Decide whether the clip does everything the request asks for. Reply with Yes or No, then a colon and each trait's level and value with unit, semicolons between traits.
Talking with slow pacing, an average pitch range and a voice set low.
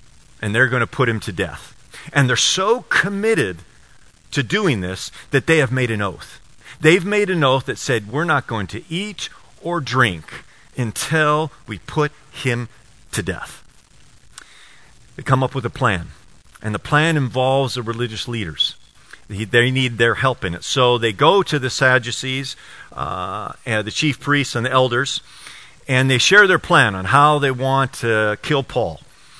No: average, 175 wpm; average, 4.2 semitones; low, 130 Hz